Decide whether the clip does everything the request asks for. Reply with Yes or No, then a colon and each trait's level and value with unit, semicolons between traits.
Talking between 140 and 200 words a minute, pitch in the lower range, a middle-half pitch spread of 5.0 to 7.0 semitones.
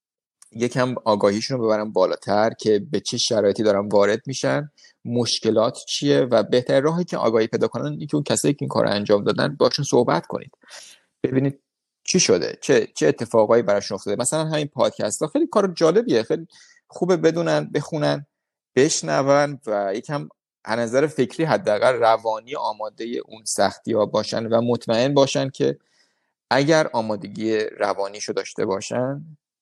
Yes: average, 150 wpm; low, 130 Hz; wide, 5.6 semitones